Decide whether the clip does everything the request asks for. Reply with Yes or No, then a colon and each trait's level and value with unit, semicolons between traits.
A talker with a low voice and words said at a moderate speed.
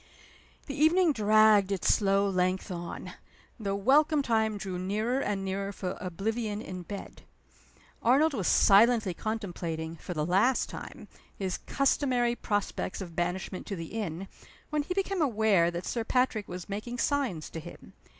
No: high, 205 Hz; average, 150 wpm